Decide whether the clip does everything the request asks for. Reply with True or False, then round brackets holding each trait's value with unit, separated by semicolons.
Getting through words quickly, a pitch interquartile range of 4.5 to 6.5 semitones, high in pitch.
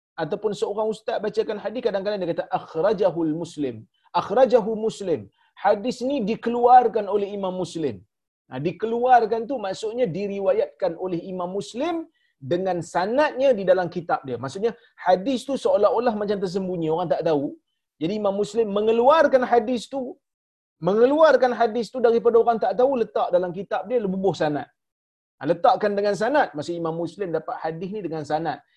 True (150 wpm; 5.2 semitones; 205 Hz)